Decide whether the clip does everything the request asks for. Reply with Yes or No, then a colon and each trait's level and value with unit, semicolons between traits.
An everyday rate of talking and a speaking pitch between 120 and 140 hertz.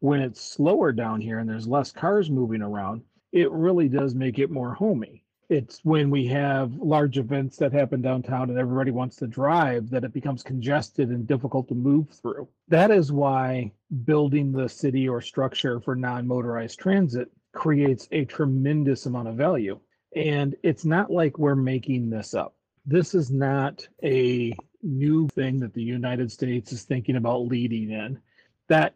Yes: average, 170 wpm; low, 135 Hz